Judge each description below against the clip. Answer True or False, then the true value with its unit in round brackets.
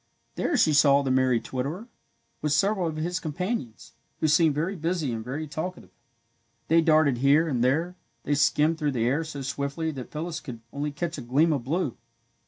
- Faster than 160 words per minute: True (190 wpm)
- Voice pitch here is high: False (150 Hz)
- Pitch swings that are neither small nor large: True (3.2 semitones)